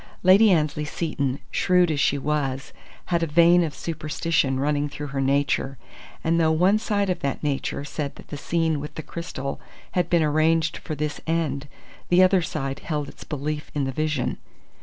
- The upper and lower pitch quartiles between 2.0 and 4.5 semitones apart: Yes, average, 2.8 semitones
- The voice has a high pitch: No, medium, 155 Hz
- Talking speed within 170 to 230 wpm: Yes, average, 180 wpm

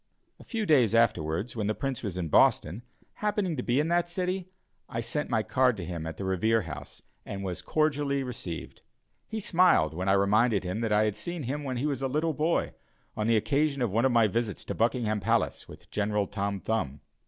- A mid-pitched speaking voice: No, low, 115 Hz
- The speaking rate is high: Yes, fast, 215 wpm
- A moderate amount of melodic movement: No, wide, 6.5 semitones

